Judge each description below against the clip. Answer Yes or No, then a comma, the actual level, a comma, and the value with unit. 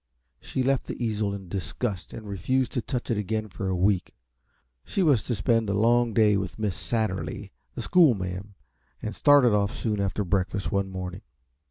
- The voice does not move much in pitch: No, average, 3.6 semitones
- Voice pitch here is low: Yes, low, 105 Hz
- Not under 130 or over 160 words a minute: No, average, 180 wpm